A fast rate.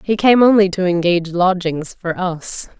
No: average, 170 wpm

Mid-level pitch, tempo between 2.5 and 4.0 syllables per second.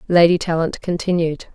No: medium, 170 Hz; 5.2 syllables/s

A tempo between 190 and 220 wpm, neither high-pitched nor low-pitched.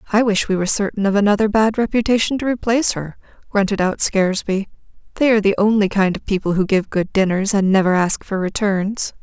No: average, 200 wpm; high, 205 Hz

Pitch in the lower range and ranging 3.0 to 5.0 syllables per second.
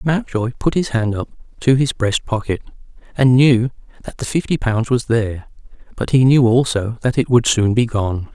Yes: low, 120 Hz; 4.9 syllables/s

